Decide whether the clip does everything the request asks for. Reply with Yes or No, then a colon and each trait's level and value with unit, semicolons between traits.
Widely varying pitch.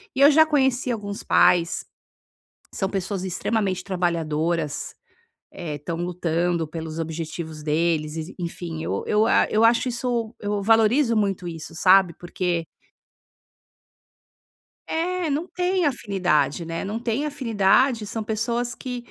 Yes: wide, 6.0 semitones